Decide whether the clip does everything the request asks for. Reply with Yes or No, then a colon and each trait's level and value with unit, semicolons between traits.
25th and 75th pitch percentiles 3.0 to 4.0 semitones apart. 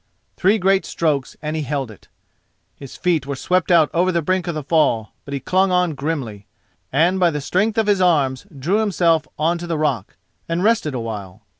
No: average, 4.7 semitones